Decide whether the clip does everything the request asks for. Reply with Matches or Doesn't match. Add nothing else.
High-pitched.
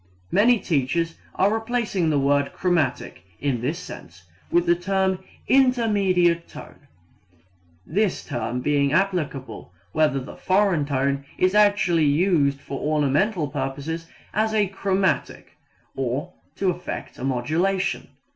Doesn't match